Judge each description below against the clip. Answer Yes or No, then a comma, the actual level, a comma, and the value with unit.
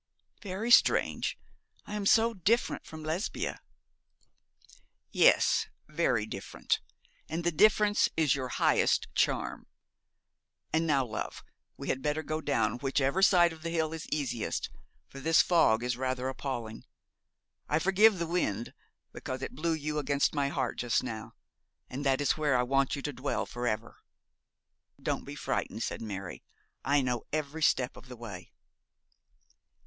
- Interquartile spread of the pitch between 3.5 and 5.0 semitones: Yes, average, 4.5 semitones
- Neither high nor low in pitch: Yes, medium, 145 Hz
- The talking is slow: No, average, 150 wpm